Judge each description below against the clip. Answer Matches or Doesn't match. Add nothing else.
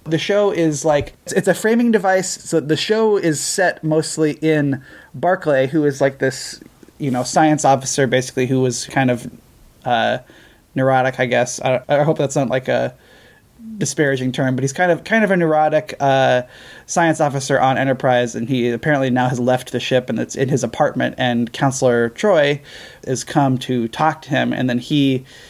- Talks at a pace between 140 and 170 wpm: Doesn't match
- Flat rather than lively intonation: Doesn't match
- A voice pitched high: Doesn't match